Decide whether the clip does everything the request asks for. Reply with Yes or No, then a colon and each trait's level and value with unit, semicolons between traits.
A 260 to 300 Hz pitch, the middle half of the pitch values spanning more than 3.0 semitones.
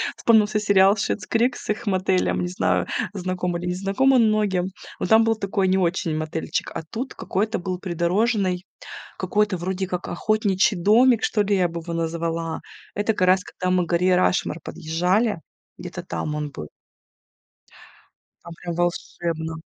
No: medium, 185 Hz; average, 3.5 semitones